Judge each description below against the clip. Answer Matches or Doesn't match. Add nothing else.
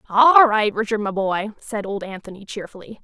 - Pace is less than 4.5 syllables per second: Doesn't match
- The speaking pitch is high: Matches